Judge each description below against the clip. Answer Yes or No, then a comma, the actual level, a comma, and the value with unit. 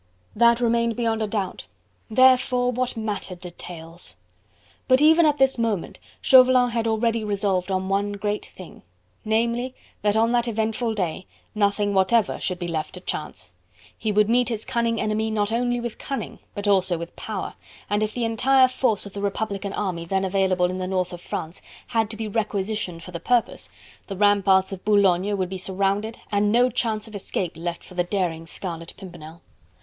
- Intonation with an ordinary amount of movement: Yes, average, 3.6 semitones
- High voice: Yes, high, 205 Hz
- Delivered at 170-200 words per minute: Yes, average, 180 wpm